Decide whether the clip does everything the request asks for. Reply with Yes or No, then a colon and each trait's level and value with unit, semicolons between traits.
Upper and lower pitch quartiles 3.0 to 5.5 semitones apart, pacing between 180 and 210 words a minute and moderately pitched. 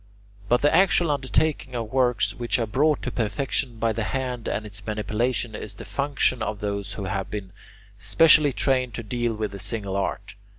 No: average, 3.8 semitones; average, 185 wpm; low, 115 Hz